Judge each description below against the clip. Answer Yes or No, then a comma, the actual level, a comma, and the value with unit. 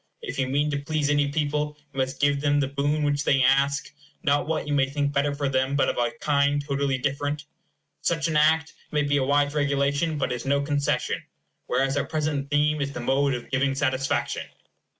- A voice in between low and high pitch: Yes, medium, 145 Hz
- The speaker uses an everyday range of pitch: No, narrow, 1.1 semitones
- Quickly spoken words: Yes, fast, 210 wpm